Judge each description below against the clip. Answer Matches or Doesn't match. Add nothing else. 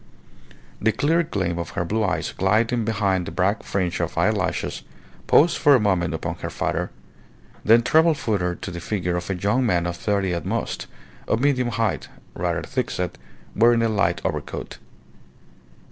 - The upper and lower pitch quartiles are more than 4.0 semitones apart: Matches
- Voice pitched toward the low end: Matches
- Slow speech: Doesn't match